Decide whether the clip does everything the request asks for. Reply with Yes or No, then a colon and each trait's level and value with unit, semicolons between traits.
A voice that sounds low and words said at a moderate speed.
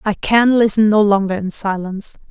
No: high, 205 Hz; average, 180 wpm